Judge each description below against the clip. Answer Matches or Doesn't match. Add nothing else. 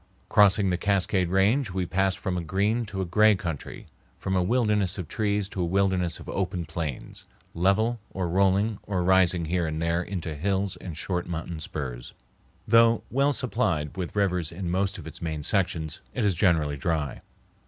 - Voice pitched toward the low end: Matches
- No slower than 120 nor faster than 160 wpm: Doesn't match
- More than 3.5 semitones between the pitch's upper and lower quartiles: Doesn't match